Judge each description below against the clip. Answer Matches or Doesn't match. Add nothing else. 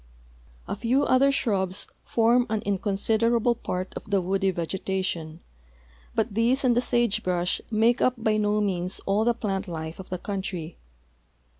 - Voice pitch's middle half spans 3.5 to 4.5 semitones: Matches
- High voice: Matches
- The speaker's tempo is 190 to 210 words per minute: Doesn't match